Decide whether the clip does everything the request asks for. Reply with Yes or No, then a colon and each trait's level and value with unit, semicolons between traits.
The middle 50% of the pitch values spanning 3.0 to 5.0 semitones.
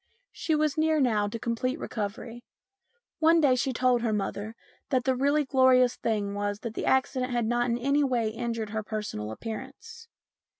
Yes: average, 3.4 semitones